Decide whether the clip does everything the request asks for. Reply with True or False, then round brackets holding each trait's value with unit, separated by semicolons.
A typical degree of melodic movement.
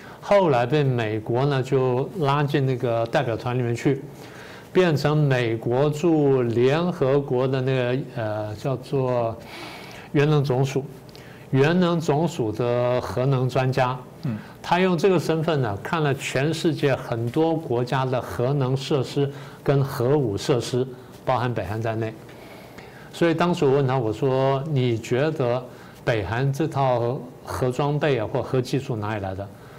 True (3.1 semitones)